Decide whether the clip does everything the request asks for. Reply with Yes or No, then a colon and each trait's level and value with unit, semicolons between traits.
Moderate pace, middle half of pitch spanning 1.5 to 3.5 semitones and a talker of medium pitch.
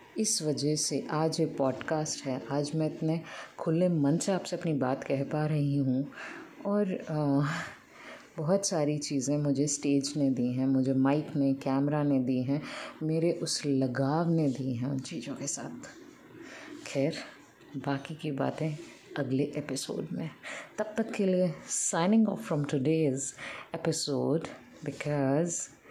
Yes: average, 150 wpm; average, 3.2 semitones; medium, 150 Hz